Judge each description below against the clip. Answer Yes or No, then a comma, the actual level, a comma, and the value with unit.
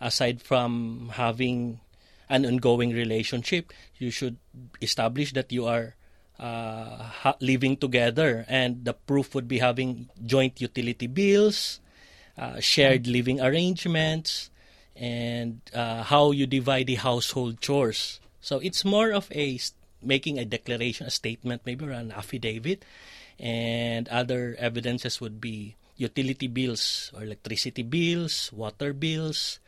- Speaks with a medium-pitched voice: No, low, 125 Hz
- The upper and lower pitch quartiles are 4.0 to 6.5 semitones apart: No, narrow, 2.6 semitones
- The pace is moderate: Yes, average, 130 wpm